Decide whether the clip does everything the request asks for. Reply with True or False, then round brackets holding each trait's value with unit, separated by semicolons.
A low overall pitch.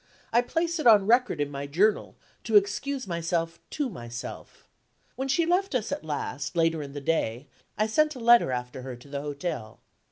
False (175 Hz)